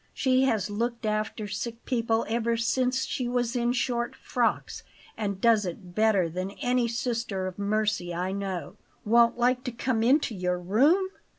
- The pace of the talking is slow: No, average, 165 wpm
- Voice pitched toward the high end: Yes, high, 230 Hz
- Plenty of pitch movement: No, average, 3.4 semitones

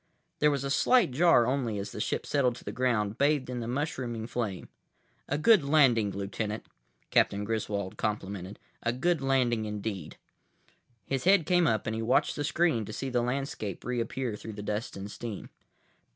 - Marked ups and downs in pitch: No, average, 4.7 semitones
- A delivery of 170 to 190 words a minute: Yes, average, 180 wpm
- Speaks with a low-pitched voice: Yes, low, 120 Hz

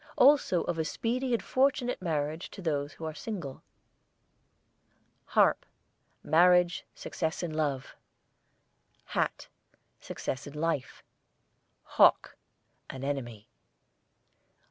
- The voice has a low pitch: No, medium, 160 Hz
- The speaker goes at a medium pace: No, slow, 100 wpm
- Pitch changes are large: No, average, 4.3 semitones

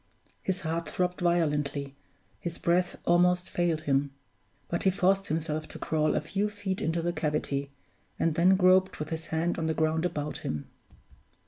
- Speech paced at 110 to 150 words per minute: No, average, 165 wpm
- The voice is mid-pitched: Yes, medium, 165 Hz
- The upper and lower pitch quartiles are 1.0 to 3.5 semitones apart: Yes, average, 2.7 semitones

